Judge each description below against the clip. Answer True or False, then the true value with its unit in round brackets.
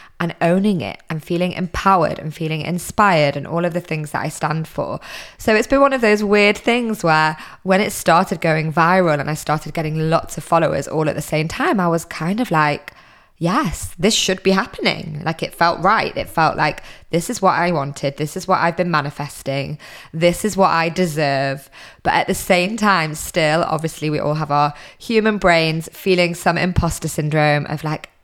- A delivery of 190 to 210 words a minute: True (205 wpm)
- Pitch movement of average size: True (3.4 semitones)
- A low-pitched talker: False (165 Hz)